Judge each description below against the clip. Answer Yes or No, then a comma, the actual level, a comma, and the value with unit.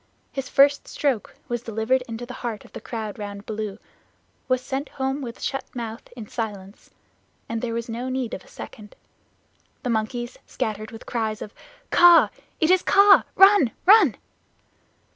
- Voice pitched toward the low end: No, high, 240 Hz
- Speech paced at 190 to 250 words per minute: No, average, 165 wpm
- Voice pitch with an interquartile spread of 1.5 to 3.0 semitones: No, average, 3.5 semitones